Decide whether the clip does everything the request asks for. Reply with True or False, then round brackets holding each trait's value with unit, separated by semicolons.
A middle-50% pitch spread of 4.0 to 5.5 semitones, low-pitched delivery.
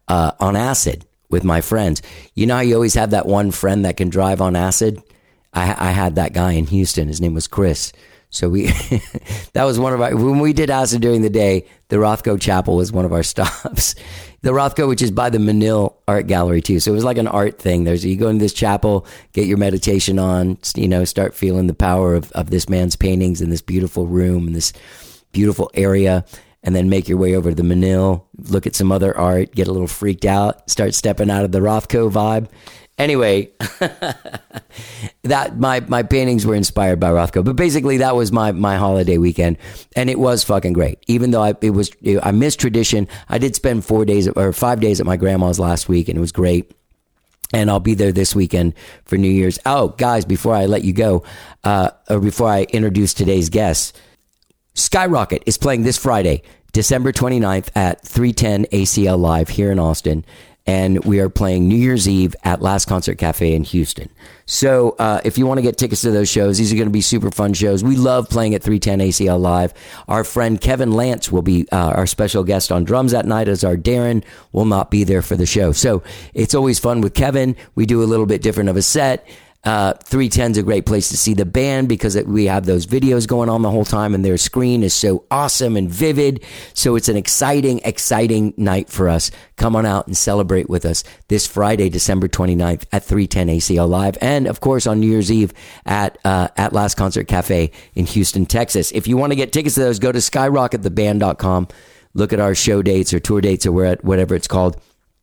False (3.5 semitones; 100 Hz)